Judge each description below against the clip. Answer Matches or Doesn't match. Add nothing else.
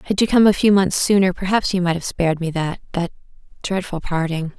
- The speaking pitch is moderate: Matches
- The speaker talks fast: Matches